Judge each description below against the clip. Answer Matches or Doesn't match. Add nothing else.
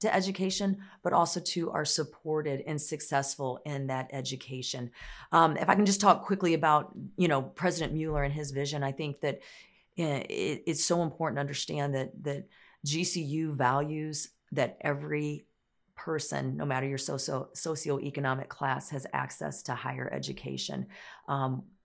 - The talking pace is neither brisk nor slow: Matches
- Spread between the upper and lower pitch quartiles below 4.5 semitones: Matches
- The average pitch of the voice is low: Doesn't match